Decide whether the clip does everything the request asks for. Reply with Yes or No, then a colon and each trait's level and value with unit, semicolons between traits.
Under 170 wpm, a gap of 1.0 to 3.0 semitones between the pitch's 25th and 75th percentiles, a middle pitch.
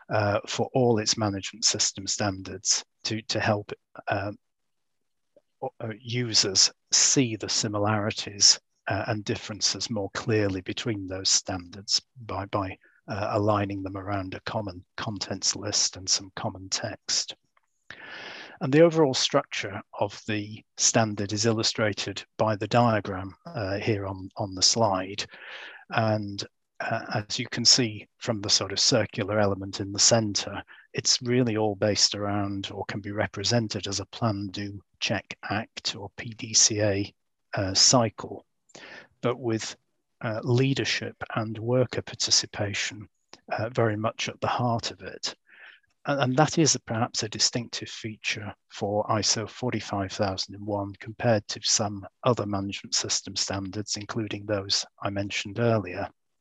No: slow, 135 wpm; narrow, 2.5 semitones; low, 105 Hz